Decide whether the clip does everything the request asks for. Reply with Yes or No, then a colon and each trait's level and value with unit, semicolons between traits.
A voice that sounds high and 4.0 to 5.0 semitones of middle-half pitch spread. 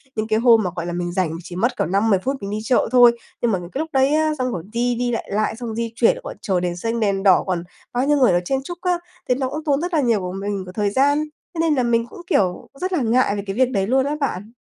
No: high, 230 Hz; wide, 5.4 semitones